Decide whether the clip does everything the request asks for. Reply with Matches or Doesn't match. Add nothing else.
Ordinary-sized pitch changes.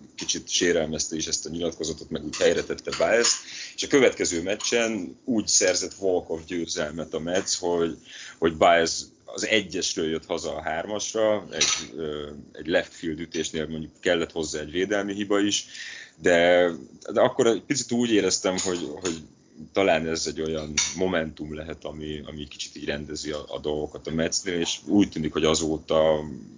Matches